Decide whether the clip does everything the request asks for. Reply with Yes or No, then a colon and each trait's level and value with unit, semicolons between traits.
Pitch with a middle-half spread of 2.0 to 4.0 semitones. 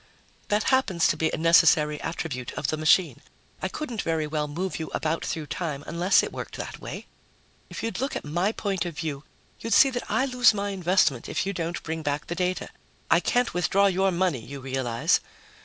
No: average, 4.6 semitones